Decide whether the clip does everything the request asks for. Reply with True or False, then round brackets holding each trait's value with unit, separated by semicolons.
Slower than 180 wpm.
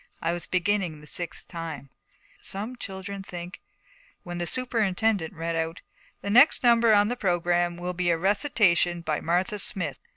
True (165 wpm)